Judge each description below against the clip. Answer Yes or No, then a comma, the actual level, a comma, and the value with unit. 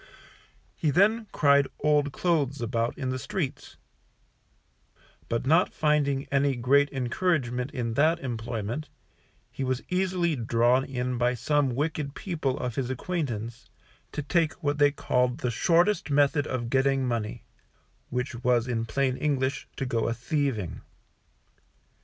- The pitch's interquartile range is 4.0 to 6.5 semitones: No, average, 3.4 semitones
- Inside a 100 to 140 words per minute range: Yes, slow, 135 wpm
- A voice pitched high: No, low, 135 Hz